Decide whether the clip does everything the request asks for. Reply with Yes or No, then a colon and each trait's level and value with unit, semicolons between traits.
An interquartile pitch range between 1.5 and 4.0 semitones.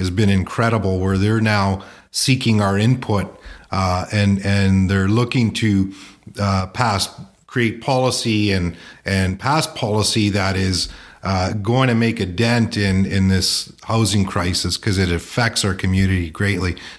Yes: average, 2.9 semitones